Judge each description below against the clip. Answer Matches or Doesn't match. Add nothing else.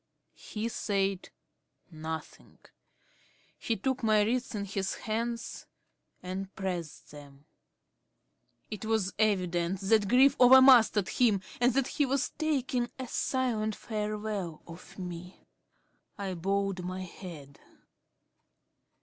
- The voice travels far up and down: Doesn't match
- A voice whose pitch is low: Doesn't match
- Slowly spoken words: Matches